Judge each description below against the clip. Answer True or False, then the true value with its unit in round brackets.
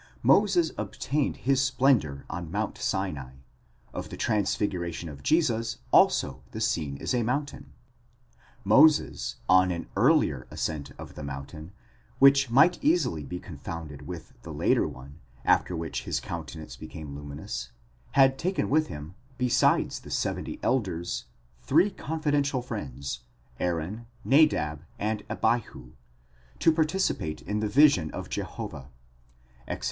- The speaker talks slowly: True (130 wpm)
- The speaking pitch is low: True (100 Hz)